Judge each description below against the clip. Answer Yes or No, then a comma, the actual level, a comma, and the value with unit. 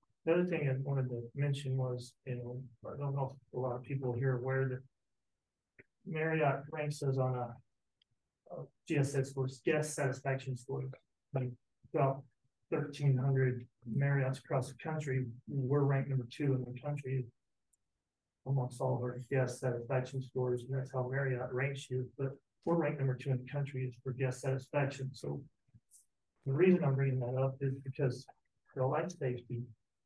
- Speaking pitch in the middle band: No, low, 130 Hz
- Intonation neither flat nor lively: No, narrow, 1.7 semitones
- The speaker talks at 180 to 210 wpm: No, average, 170 wpm